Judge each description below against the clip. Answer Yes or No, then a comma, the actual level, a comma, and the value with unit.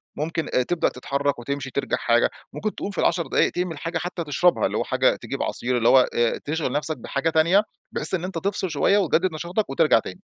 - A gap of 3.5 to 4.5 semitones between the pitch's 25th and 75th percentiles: Yes, average, 4.2 semitones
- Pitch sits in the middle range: Yes, medium, 160 Hz